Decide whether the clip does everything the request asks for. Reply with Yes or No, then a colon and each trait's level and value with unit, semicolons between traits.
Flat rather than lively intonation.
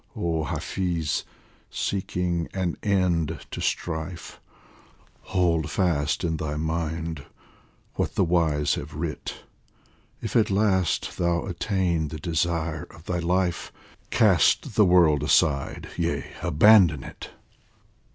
Yes: narrow, 2.3 semitones